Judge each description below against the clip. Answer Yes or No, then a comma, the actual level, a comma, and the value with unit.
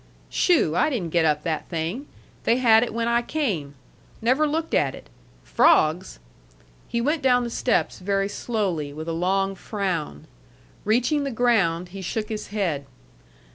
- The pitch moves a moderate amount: No, wide, 6.4 semitones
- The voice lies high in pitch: Yes, high, 205 Hz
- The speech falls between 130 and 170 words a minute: Yes, average, 160 wpm